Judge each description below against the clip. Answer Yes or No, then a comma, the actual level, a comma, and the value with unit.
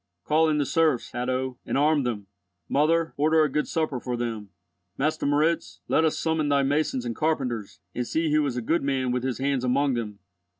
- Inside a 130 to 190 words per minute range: No, fast, 205 wpm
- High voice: No, medium, 140 Hz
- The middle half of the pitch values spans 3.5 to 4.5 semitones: Yes, average, 3.8 semitones